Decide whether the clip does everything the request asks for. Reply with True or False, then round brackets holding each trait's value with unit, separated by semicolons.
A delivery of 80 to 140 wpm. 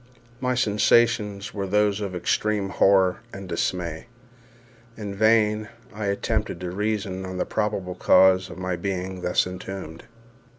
True (135 wpm)